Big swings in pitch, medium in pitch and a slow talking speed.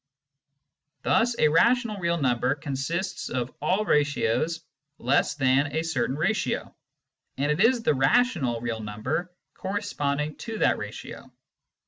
Yes: wide, 6.3 semitones; medium, 150 Hz; slow, 125 wpm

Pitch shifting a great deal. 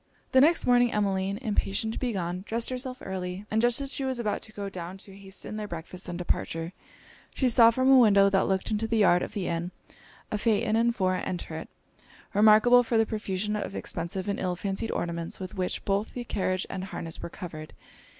No: average, 3.6 semitones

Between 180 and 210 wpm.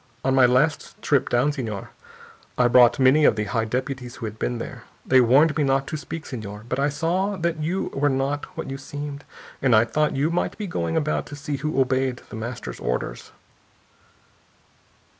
Yes: average, 195 wpm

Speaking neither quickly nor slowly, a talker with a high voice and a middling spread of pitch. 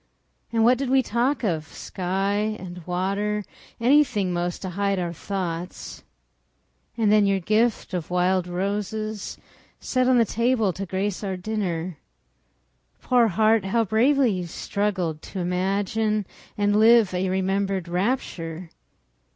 No: slow, 130 wpm; high, 200 Hz; average, 3.3 semitones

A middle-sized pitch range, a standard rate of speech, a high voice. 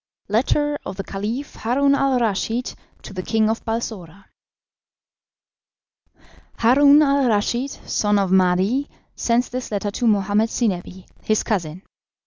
No: average, 4.3 semitones; slow, 125 wpm; high, 225 Hz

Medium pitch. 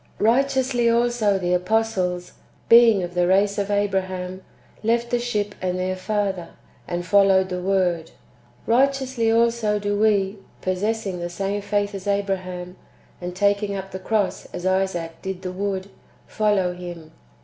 No: high, 195 Hz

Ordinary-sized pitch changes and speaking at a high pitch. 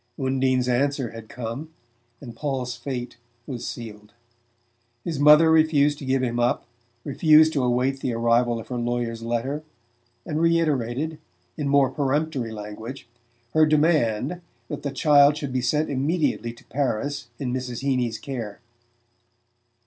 No: average, 3.7 semitones; low, 130 Hz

